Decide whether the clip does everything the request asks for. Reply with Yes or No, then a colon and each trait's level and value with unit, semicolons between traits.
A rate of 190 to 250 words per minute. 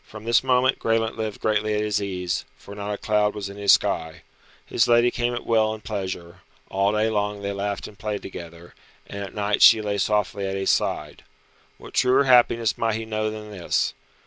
Yes: fast, 205 wpm